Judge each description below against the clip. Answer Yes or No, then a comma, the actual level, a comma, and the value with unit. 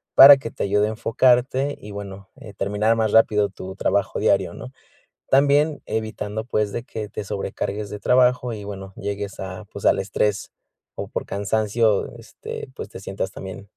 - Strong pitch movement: No, narrow, 2.4 semitones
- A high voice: No, low, 105 Hz